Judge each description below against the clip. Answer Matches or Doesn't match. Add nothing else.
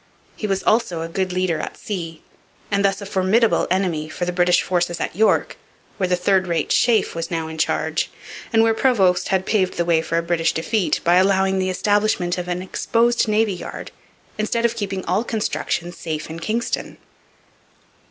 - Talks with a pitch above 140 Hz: Matches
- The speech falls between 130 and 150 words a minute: Doesn't match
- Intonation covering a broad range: Doesn't match